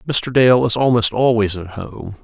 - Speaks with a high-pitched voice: No, low, 115 Hz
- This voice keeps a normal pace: Yes, average, 190 wpm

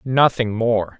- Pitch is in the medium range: No, low, 110 Hz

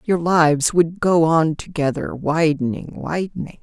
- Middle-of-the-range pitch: Yes, medium, 160 Hz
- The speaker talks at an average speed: No, slow, 130 wpm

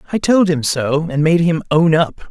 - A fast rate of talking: Yes, fast, 235 wpm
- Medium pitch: Yes, medium, 160 Hz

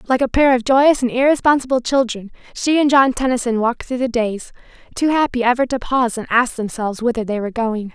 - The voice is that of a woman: Yes, female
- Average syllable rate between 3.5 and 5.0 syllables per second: No, 6.0 syllables/s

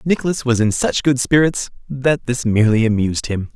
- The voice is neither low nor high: No, low, 125 Hz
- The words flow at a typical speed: Yes, average, 185 wpm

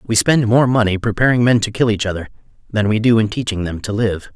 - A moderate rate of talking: No, fast, 250 wpm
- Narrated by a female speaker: No, male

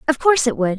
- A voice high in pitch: Yes, very high, 260 Hz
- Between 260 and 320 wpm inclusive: Yes, fast, 305 wpm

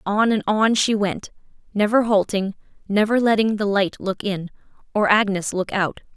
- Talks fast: No, average, 165 wpm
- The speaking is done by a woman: Yes, female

